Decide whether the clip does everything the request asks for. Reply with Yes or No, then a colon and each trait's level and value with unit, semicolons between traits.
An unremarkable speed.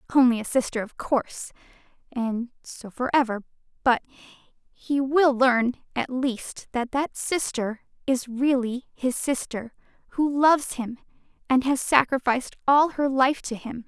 Yes: average, 145 wpm